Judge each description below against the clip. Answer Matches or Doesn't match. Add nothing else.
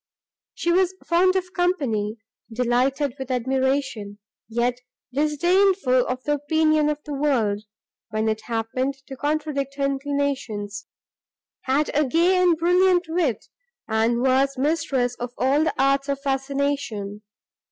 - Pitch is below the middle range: Doesn't match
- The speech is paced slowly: Matches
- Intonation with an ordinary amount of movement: Matches